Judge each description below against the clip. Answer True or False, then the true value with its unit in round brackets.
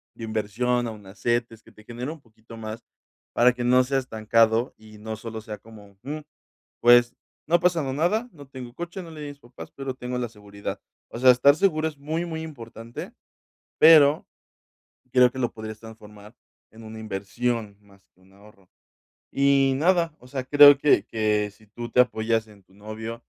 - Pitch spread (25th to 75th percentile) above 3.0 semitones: True (4.2 semitones)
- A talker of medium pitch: False (120 Hz)